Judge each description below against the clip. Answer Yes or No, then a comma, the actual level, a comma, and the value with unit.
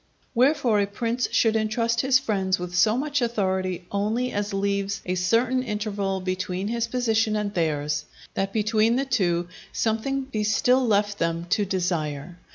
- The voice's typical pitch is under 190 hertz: No, high, 210 Hz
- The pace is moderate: Yes, average, 160 wpm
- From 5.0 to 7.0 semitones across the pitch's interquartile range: No, average, 3.9 semitones